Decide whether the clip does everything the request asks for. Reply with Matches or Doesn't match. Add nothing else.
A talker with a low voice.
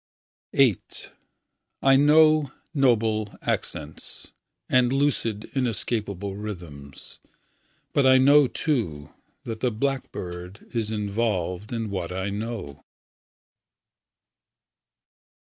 Matches